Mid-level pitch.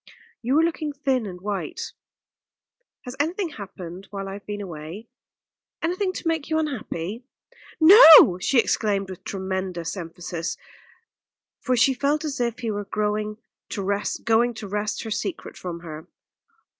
No: high, 210 Hz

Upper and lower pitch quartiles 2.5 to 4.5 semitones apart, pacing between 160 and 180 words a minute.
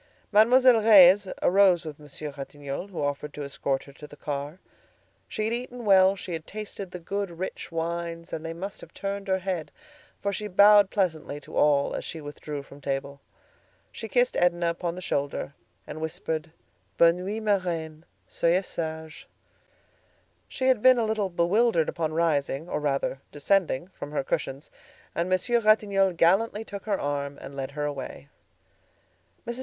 No: average, 5.2 semitones; average, 170 wpm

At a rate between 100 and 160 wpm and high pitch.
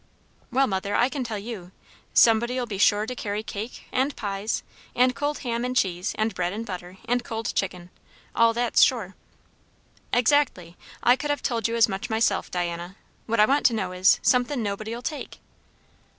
No: average, 180 wpm; high, 225 Hz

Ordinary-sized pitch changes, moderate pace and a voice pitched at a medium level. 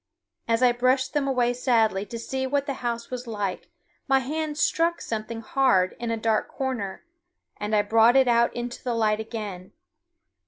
No: average, 3.1 semitones; average, 180 wpm; high, 235 Hz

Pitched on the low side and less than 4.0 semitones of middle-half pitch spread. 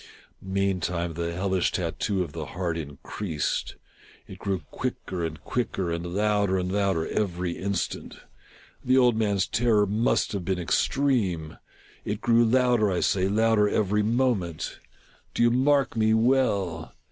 No: low, 100 Hz; average, 4.3 semitones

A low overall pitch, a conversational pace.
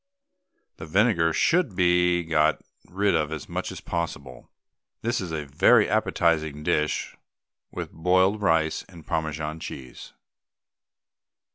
No: very low, 80 Hz; slow, 120 wpm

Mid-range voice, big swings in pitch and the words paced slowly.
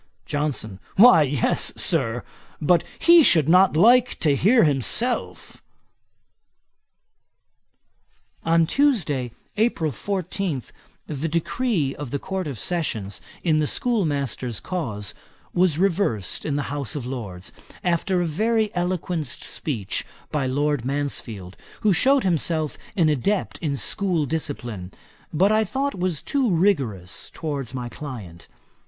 Yes: medium, 155 Hz; wide, 6.0 semitones; slow, 125 wpm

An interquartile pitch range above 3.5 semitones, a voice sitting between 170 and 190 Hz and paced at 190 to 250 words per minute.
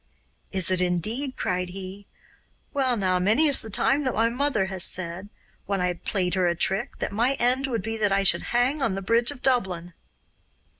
No: average, 5.1 semitones; high, 205 Hz; average, 200 wpm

